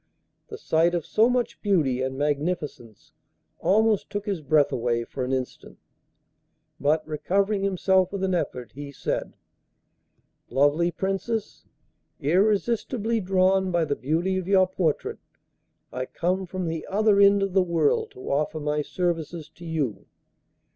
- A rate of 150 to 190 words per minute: No, average, 140 wpm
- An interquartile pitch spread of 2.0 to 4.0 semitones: No, average, 4.7 semitones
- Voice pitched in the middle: Yes, medium, 175 Hz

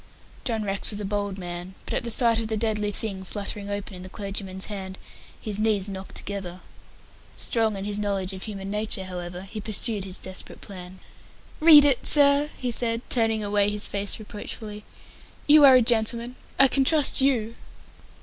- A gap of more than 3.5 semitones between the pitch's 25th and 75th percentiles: No, average, 2.9 semitones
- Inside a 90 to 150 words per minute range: No, average, 180 wpm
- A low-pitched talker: No, high, 210 Hz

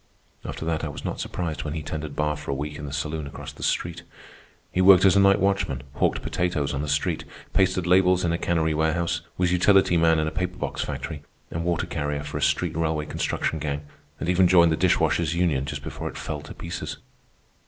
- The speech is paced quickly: Yes, fast, 220 wpm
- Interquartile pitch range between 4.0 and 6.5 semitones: No, average, 2.8 semitones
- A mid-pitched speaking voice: No, very low, 80 Hz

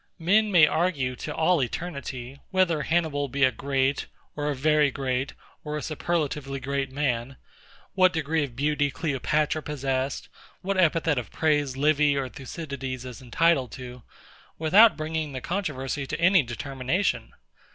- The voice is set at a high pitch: No, medium, 145 Hz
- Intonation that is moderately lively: Yes, average, 3.3 semitones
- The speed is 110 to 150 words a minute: Yes, average, 145 wpm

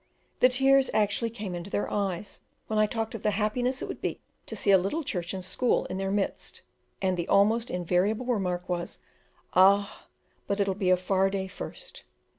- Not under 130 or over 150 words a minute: No, average, 195 wpm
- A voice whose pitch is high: Yes, high, 200 Hz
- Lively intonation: No, average, 3.1 semitones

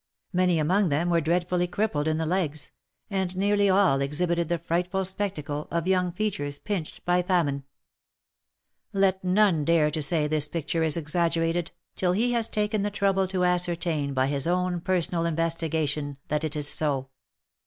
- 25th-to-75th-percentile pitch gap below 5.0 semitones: Yes, average, 3.4 semitones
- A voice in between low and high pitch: Yes, medium, 170 Hz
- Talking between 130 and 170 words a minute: Yes, average, 165 wpm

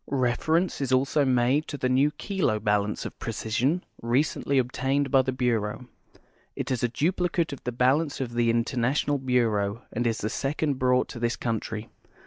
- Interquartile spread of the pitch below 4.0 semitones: Yes, average, 3.2 semitones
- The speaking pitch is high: No, low, 125 Hz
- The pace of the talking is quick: No, average, 175 wpm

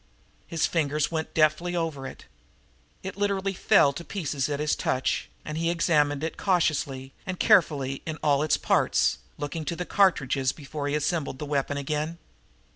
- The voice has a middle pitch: Yes, medium, 155 Hz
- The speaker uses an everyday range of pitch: Yes, average, 3.1 semitones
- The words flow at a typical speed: Yes, average, 165 wpm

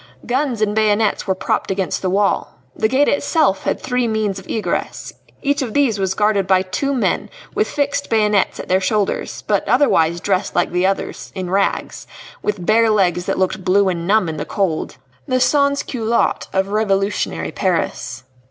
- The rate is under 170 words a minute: No, average, 180 wpm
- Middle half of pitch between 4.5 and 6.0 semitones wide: No, average, 3.4 semitones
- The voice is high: Yes, high, 205 Hz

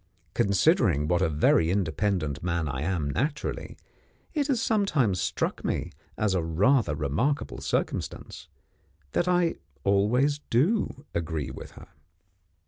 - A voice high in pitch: No, low, 100 Hz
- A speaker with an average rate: No, slow, 125 wpm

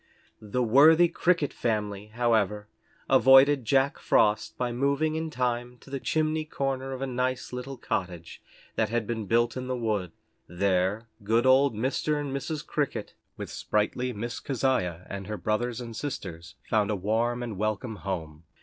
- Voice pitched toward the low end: Yes, low, 120 Hz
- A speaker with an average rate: Yes, average, 160 wpm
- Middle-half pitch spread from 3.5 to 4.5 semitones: Yes, average, 4.2 semitones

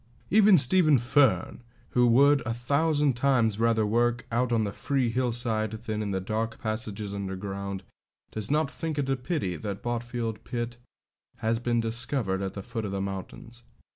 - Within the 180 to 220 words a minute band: No, average, 170 wpm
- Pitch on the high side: No, low, 115 Hz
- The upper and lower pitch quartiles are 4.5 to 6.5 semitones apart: No, average, 3.4 semitones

